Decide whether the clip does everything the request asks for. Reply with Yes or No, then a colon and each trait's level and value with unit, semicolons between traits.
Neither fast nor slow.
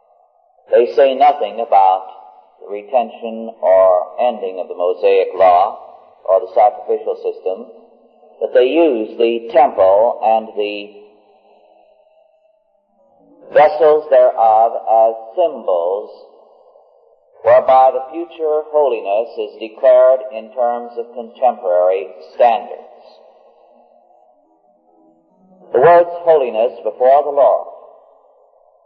No: slow, 90 wpm